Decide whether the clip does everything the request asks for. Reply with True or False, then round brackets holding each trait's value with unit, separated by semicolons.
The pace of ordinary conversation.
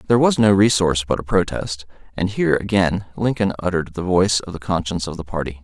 False (215 wpm)